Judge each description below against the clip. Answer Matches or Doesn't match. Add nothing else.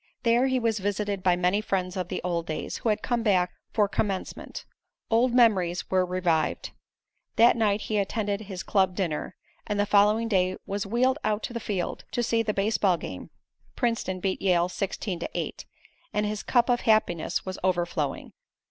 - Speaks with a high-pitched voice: Matches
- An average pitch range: Matches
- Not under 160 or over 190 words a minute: Matches